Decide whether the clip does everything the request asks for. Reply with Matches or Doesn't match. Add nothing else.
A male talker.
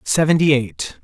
Matches